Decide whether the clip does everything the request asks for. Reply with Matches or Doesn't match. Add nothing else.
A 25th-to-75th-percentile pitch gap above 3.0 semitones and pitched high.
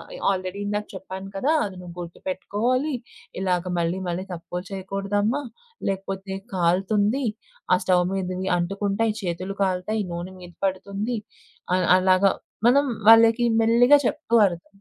Doesn't match